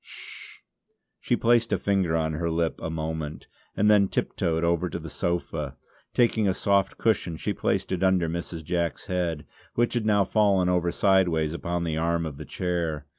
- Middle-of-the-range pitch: No, very low, 85 Hz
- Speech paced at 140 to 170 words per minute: No, average, 180 wpm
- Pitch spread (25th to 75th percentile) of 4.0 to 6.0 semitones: No, average, 3.0 semitones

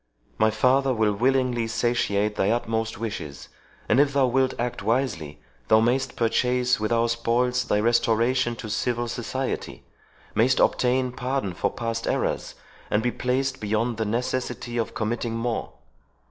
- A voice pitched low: Yes, low, 120 Hz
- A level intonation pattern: Yes, narrow, 2.2 semitones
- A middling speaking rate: Yes, average, 145 wpm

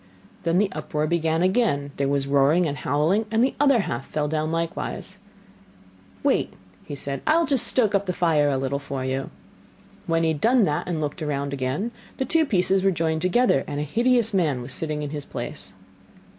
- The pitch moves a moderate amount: No, wide, 5.8 semitones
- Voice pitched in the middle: Yes, medium, 160 Hz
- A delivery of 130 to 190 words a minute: No, fast, 205 wpm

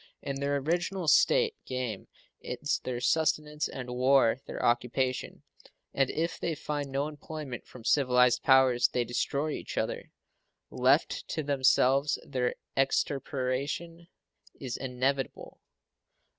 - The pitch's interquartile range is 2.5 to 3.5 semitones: Yes, average, 3.0 semitones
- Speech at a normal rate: No, slow, 115 wpm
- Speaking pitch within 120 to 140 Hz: Yes, low, 135 Hz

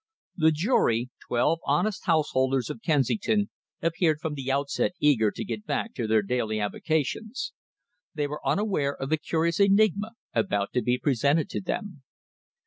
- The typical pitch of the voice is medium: Yes, medium, 150 Hz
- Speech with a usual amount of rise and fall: No, wide, 6.7 semitones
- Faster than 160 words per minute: No, average, 150 wpm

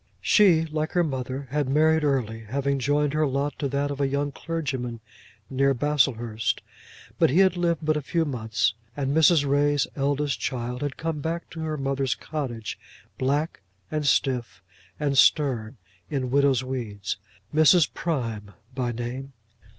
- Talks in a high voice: No, medium, 140 Hz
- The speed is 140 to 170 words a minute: Yes, average, 155 wpm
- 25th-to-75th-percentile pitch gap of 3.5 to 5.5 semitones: No, average, 3.0 semitones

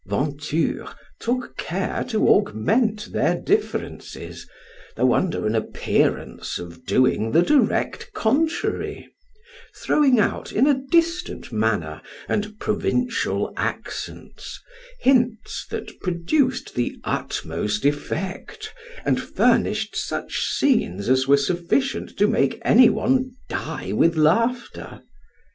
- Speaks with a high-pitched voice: Yes, high, 210 Hz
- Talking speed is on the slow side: Yes, slow, 105 wpm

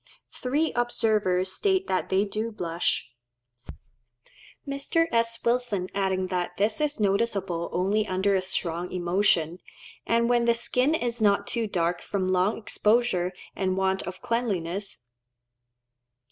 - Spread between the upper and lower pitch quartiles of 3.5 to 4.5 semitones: Yes, average, 4.1 semitones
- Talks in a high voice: Yes, high, 200 Hz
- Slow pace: Yes, slow, 130 wpm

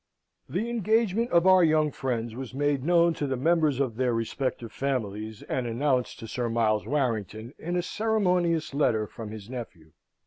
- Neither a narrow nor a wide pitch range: No, wide, 6.7 semitones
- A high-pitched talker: No, low, 135 Hz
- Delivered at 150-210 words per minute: Yes, average, 170 wpm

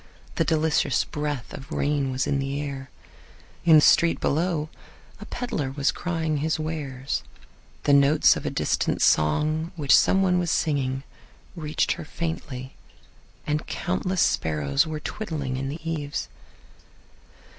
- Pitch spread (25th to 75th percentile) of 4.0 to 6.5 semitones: No, average, 2.8 semitones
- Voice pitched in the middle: Yes, medium, 150 Hz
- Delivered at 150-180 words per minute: No, average, 140 wpm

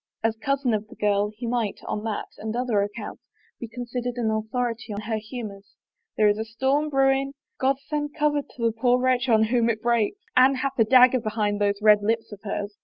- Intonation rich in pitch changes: No, average, 3.1 semitones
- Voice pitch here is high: Yes, high, 230 Hz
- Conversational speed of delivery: No, fast, 220 wpm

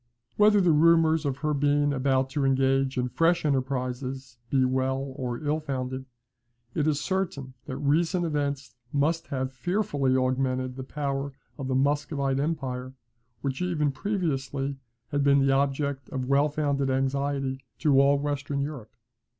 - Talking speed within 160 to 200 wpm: No, average, 150 wpm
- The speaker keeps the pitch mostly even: Yes, narrow, 2.0 semitones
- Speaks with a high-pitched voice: No, medium, 140 Hz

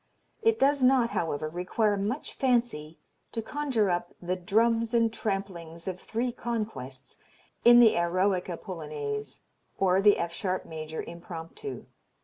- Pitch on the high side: Yes, high, 195 Hz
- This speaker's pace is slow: Yes, slow, 130 wpm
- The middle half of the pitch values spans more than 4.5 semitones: Yes, wide, 5.5 semitones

